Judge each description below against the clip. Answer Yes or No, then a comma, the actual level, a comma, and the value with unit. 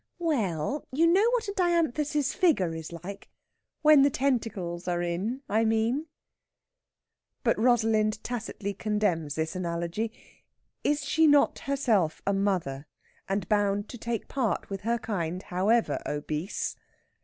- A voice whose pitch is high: Yes, high, 215 Hz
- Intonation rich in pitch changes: Yes, wide, 7.3 semitones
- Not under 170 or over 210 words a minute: No, slow, 135 wpm